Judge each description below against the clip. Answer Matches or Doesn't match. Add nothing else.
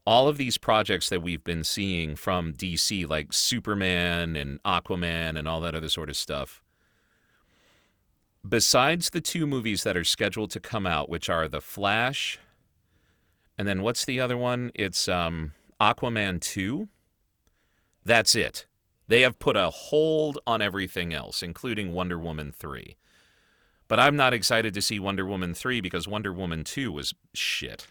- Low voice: Matches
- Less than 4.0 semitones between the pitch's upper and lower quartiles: Doesn't match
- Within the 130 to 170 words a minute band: Matches